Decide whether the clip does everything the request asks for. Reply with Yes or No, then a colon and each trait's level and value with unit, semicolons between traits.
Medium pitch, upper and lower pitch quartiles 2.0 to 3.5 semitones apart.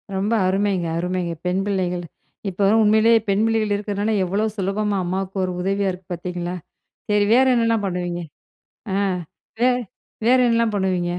No: high, 195 Hz; average, 2.9 semitones